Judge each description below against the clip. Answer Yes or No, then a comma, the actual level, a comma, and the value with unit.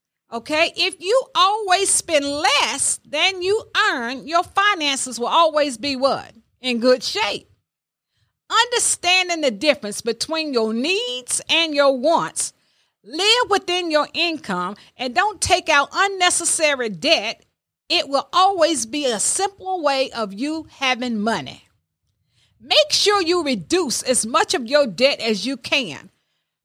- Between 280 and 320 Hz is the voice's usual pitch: Yes, very high, 305 Hz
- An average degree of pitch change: No, wide, 6.1 semitones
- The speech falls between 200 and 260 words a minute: No, slow, 135 wpm